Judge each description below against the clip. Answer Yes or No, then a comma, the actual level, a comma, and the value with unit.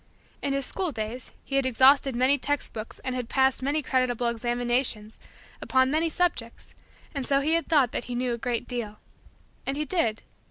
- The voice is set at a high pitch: Yes, very high, 260 Hz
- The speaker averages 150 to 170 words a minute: No, average, 190 wpm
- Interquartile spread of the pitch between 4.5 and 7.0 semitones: No, narrow, 2.6 semitones